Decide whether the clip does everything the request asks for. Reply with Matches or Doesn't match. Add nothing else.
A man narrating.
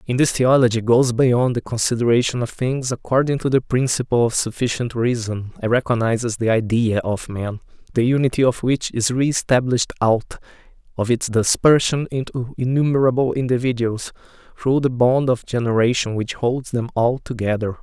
Matches